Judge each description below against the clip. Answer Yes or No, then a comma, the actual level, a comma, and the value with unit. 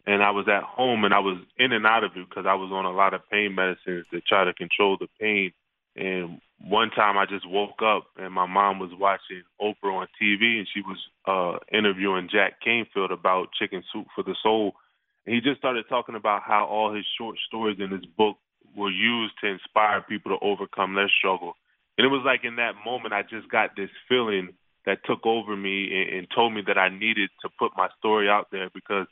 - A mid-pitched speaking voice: No, low, 100 Hz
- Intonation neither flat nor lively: No, narrow, 2.3 semitones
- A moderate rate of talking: No, fast, 225 wpm